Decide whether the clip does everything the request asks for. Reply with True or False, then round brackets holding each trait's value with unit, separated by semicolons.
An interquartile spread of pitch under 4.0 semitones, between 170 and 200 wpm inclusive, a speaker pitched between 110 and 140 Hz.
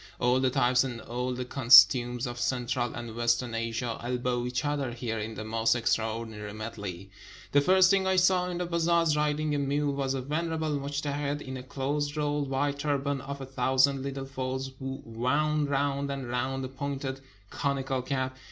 True (2.8 semitones; 180 wpm; 135 Hz)